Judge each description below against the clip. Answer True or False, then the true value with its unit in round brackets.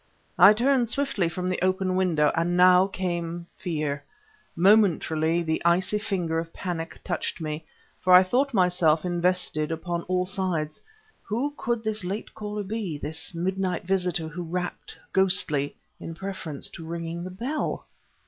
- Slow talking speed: False (150 wpm)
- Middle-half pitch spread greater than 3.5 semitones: False (2.7 semitones)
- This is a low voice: False (180 Hz)